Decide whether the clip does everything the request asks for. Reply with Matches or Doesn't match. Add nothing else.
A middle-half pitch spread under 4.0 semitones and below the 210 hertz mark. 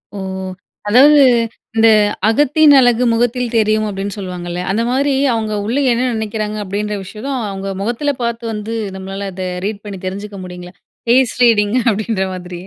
Doesn't match